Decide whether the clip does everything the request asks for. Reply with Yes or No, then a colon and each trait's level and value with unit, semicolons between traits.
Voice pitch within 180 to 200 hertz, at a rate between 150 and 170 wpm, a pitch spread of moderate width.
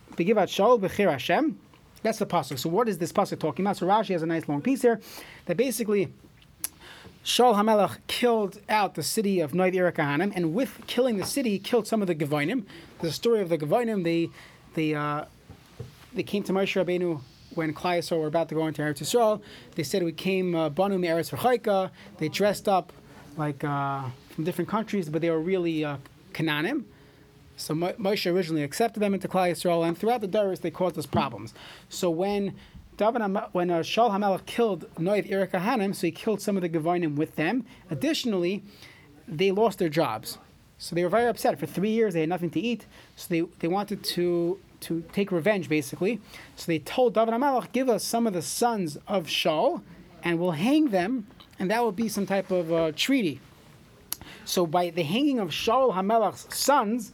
No: medium, 185 Hz; average, 185 wpm; average, 4.5 semitones